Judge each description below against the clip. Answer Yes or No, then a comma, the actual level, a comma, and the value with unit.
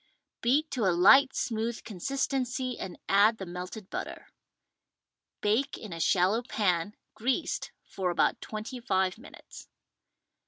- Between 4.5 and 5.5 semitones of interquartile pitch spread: Yes, average, 5.2 semitones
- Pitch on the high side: Yes, high, 215 Hz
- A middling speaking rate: No, slow, 125 wpm